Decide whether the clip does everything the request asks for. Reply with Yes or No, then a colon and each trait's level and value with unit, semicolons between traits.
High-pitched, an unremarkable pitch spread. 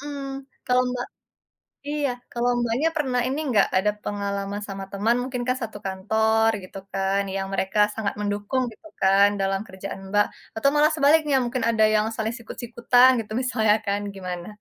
Yes: high, 220 Hz; average, 4.0 semitones